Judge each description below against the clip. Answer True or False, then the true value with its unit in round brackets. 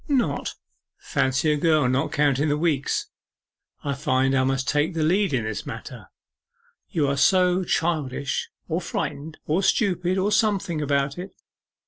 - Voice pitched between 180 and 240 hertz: False (150 Hz)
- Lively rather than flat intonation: False (4.4 semitones)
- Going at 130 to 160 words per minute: True (150 wpm)